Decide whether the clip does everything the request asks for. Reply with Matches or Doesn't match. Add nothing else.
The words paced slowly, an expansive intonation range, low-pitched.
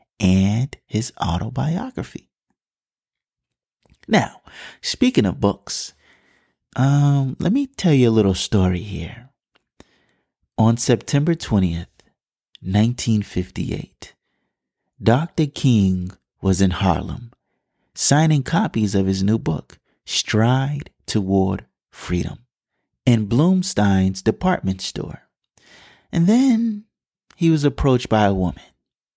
Matches